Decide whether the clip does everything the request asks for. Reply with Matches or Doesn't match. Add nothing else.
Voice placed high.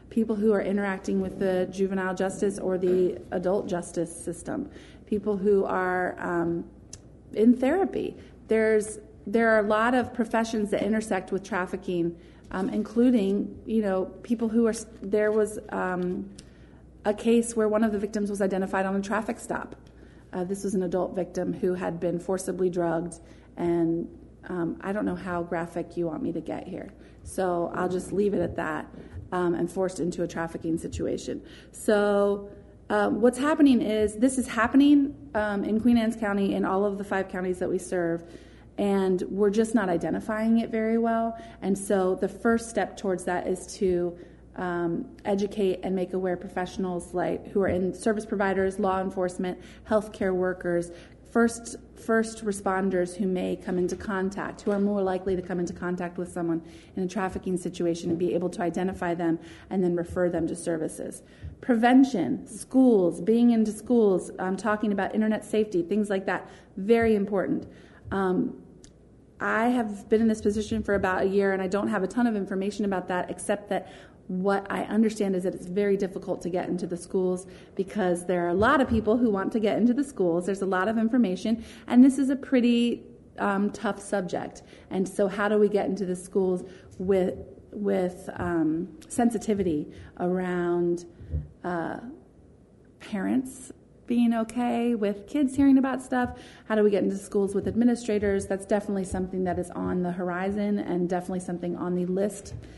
Matches